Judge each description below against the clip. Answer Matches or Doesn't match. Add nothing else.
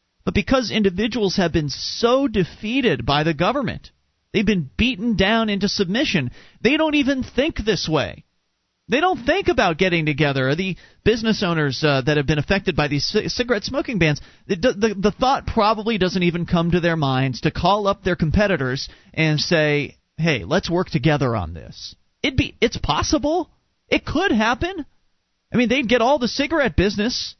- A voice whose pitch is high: Matches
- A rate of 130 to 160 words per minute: Doesn't match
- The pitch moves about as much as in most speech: Doesn't match